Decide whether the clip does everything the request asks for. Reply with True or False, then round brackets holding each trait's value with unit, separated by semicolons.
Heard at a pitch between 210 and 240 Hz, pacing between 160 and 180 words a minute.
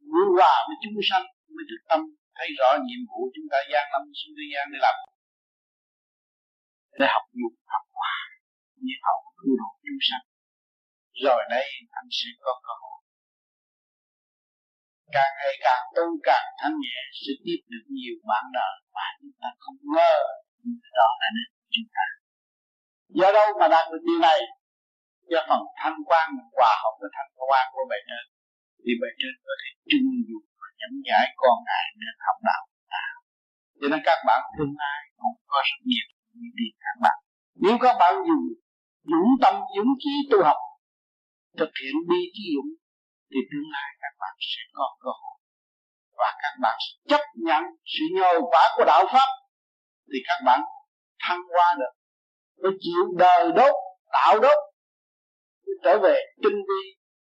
False (285 Hz; 170 wpm)